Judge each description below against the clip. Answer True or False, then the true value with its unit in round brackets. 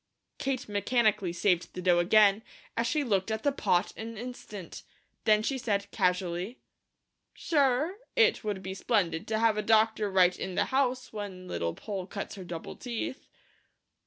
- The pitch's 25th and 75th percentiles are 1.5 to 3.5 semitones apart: False (4.4 semitones)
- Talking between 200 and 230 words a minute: False (160 wpm)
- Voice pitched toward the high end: True (210 Hz)